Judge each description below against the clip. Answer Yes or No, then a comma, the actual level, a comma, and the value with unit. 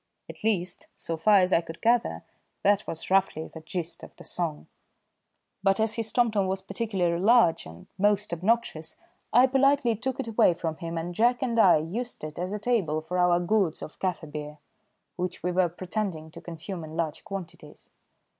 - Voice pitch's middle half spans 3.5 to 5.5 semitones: Yes, average, 4.8 semitones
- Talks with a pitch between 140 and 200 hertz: Yes, medium, 185 Hz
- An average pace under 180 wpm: No, average, 185 wpm